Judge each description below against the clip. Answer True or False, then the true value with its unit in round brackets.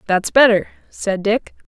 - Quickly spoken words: False (140 wpm)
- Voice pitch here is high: True (210 Hz)